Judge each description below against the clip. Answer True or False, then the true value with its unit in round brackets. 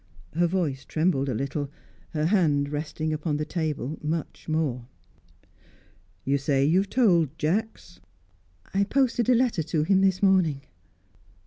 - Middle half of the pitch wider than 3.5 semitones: True (4.5 semitones)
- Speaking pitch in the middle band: True (160 Hz)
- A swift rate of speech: False (140 wpm)